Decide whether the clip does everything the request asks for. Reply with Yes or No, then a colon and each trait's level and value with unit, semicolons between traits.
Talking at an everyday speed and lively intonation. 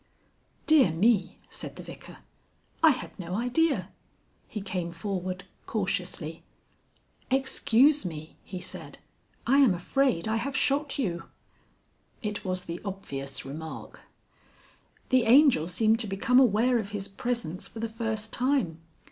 No: slow, 130 wpm; wide, 5.7 semitones